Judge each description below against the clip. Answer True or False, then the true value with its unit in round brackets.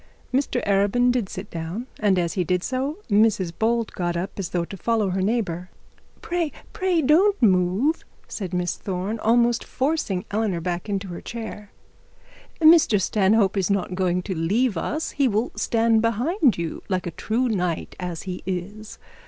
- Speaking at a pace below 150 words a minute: False (170 wpm)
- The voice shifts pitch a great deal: False (4.7 semitones)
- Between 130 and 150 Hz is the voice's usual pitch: False (205 Hz)